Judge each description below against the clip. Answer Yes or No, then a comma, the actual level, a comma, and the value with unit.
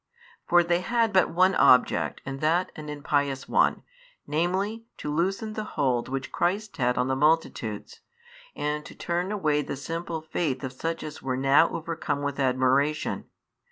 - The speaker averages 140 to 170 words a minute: Yes, average, 160 wpm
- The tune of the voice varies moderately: Yes, average, 4.3 semitones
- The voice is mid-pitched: Yes, medium, 155 Hz